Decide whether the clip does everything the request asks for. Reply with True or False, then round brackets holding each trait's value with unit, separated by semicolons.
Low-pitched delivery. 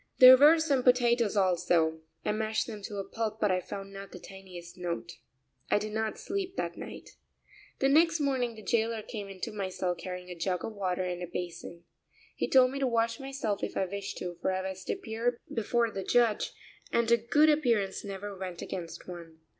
False (210 Hz)